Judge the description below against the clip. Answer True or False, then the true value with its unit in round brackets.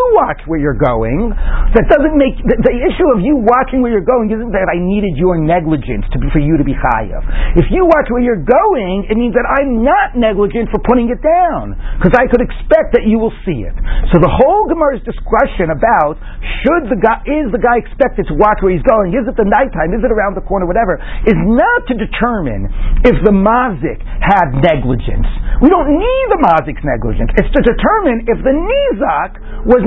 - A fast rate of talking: True (210 wpm)